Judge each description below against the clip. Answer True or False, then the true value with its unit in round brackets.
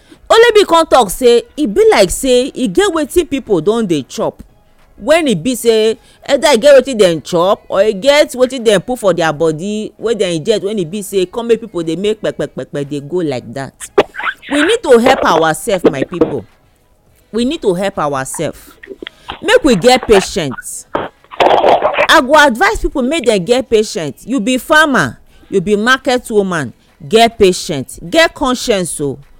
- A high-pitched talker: True (230 Hz)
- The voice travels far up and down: True (7.3 semitones)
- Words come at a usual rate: True (180 wpm)